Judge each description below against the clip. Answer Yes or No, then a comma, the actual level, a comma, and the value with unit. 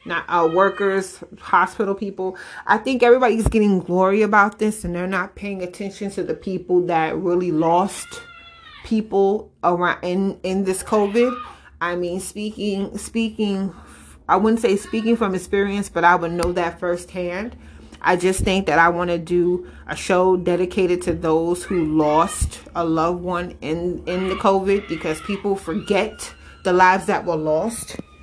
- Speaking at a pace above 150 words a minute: Yes, average, 160 wpm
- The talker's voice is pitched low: No, medium, 185 Hz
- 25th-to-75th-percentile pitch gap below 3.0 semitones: Yes, narrow, 2.5 semitones